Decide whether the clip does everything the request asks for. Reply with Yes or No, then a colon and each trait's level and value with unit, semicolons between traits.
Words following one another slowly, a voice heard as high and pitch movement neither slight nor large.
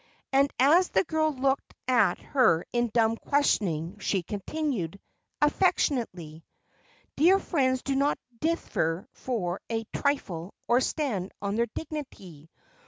No: slow, 120 wpm; high, 240 Hz; wide, 7.1 semitones